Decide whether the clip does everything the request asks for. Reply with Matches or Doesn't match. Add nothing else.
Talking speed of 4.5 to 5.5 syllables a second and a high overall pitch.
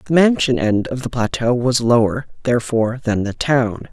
Doesn't match